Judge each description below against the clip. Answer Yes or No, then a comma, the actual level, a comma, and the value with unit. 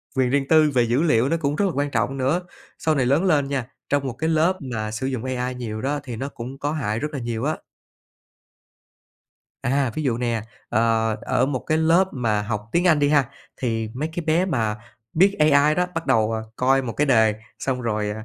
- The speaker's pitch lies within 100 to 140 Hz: Yes, low, 135 Hz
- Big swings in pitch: No, average, 4.6 semitones